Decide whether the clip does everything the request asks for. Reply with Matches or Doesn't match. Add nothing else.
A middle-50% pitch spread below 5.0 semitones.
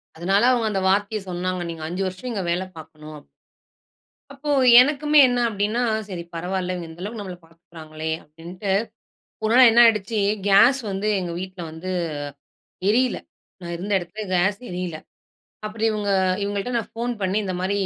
Matches